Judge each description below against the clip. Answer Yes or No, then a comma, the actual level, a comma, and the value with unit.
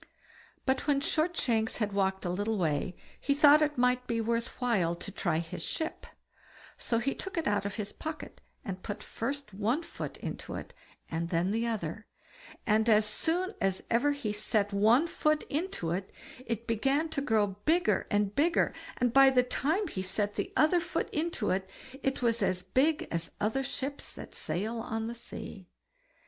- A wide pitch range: Yes, wide, 6.0 semitones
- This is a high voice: Yes, high, 230 Hz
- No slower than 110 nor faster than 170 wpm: No, average, 180 wpm